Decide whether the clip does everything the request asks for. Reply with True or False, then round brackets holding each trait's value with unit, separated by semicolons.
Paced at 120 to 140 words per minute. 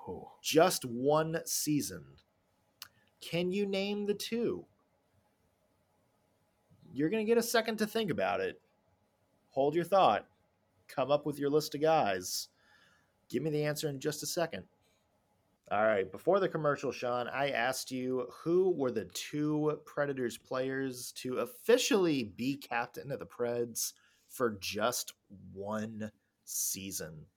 True (135 wpm)